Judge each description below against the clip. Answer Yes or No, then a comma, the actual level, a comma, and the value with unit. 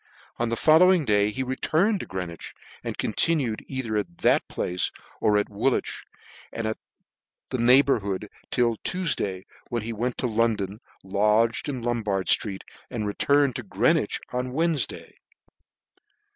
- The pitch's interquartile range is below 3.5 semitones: No, average, 4.1 semitones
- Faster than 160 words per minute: No, average, 145 wpm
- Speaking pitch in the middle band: No, low, 115 Hz